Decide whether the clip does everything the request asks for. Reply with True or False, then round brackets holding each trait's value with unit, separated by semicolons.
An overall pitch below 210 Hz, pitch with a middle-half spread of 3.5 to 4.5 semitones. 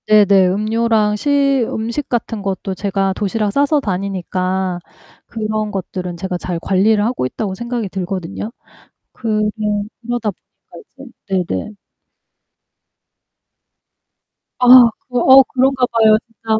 False (215 Hz; 3.8 semitones)